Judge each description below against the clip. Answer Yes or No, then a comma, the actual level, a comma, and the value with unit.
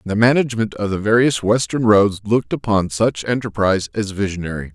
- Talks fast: No, average, 165 wpm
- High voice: No, low, 105 Hz